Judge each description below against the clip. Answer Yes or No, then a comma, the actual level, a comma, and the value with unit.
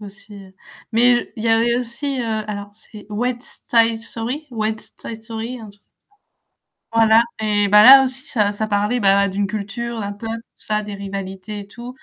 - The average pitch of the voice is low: No, high, 220 Hz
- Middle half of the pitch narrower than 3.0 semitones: Yes, narrow, 2.5 semitones